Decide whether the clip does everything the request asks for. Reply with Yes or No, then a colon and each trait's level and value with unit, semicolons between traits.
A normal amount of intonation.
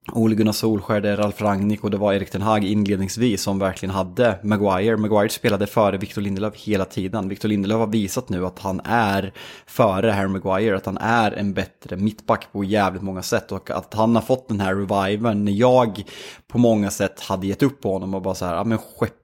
No: narrow, 2.3 semitones